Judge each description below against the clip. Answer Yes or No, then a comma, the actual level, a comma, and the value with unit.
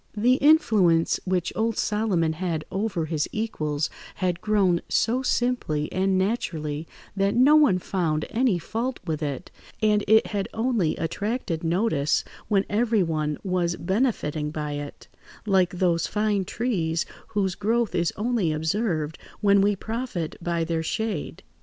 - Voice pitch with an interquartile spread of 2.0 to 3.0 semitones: No, average, 5.2 semitones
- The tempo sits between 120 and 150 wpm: Yes, average, 140 wpm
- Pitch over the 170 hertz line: Yes, high, 190 Hz